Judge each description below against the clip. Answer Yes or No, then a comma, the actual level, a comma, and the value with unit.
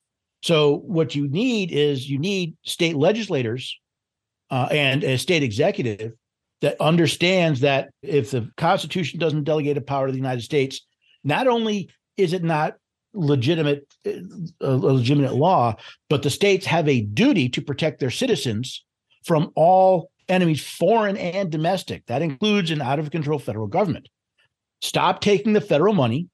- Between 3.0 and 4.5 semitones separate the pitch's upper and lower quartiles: No, average, 5.1 semitones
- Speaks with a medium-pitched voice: Yes, medium, 150 Hz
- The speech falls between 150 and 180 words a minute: Yes, average, 155 wpm